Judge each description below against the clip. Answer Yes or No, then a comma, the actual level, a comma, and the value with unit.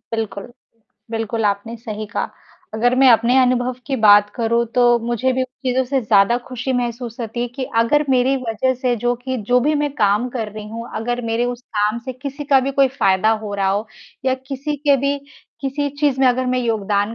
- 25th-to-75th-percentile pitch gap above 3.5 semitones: No, average, 2.8 semitones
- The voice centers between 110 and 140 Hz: No, high, 245 Hz